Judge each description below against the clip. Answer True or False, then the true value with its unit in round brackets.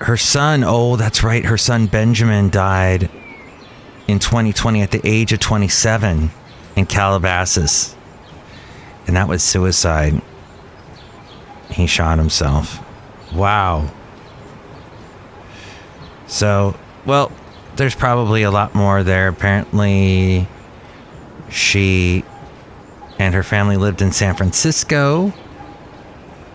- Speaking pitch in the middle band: False (100 Hz)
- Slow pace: True (95 wpm)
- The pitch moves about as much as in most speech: True (3.2 semitones)